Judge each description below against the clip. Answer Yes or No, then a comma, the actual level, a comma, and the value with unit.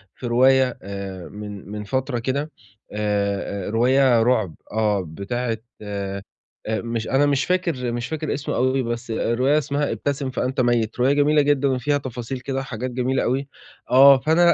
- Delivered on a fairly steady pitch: No, average, 3.7 semitones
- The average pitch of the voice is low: Yes, low, 125 Hz